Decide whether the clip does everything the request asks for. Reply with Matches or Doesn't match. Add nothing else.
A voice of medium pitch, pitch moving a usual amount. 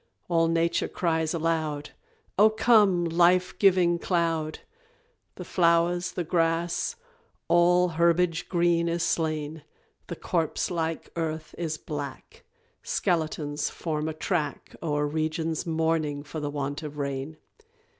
Doesn't match